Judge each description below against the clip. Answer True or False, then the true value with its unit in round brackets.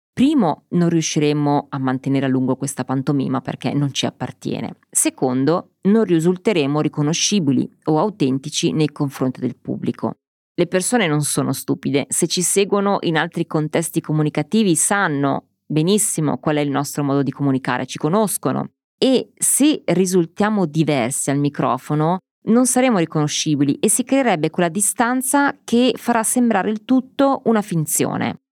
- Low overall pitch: False (160 Hz)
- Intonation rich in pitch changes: True (6.7 semitones)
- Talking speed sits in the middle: True (140 wpm)